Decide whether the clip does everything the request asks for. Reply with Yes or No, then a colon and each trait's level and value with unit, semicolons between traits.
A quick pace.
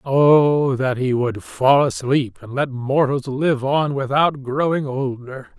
No: average, 150 wpm